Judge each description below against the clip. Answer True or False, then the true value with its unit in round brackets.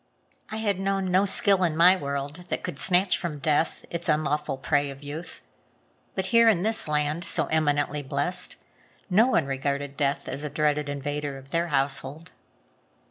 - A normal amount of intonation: True (4.1 semitones)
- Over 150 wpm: True (170 wpm)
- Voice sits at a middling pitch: True (150 Hz)